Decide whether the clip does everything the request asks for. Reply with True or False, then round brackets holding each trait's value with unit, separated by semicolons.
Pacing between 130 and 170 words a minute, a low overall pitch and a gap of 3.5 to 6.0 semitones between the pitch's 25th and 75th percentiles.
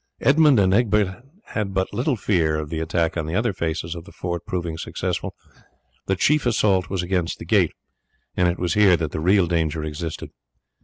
False (195 wpm; 90 Hz; 3.9 semitones)